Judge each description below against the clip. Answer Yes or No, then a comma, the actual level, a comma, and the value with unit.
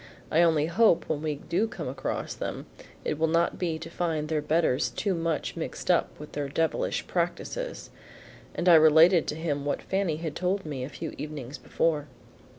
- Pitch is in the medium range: Yes, medium, 160 Hz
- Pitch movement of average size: No, narrow, 2.3 semitones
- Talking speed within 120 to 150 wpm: No, average, 185 wpm